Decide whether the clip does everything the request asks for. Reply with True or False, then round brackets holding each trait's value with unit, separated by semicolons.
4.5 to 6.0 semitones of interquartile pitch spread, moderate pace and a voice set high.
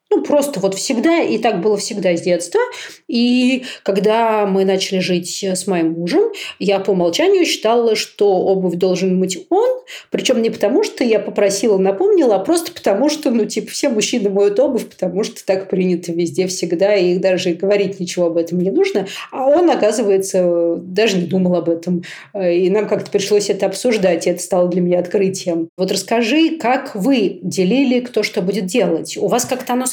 False (5.2 semitones; 180 wpm; 205 Hz)